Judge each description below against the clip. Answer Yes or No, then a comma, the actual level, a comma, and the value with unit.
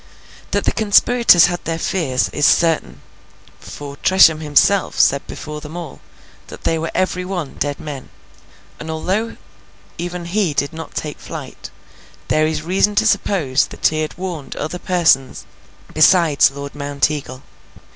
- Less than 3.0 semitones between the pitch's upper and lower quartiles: No, average, 3.9 semitones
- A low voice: No, medium, 160 Hz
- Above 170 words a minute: No, average, 145 wpm